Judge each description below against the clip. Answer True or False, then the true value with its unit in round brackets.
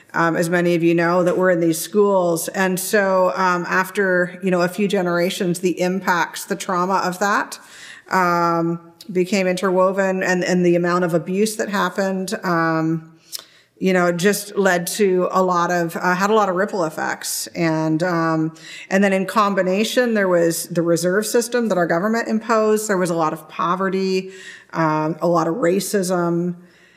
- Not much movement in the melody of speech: True (2.1 semitones)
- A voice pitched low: False (180 Hz)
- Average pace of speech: True (175 wpm)